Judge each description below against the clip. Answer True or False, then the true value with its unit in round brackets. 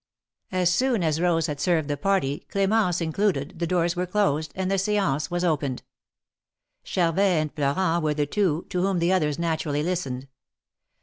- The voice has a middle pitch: True (170 Hz)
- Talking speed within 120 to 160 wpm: False (170 wpm)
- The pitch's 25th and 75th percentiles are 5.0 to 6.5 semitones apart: False (3.8 semitones)